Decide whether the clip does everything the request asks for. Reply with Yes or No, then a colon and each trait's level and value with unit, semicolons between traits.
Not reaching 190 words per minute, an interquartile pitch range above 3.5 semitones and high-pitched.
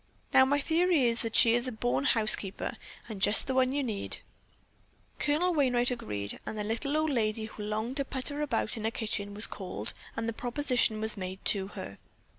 No: average, 195 wpm; average, 4.0 semitones; high, 230 Hz